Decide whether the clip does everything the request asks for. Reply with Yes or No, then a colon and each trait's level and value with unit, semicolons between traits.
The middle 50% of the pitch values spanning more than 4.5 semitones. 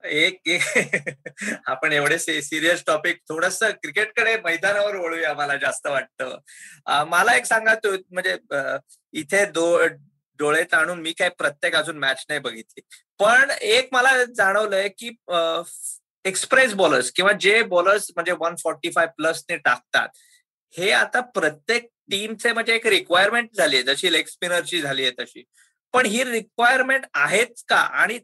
Yes: wide, 5.6 semitones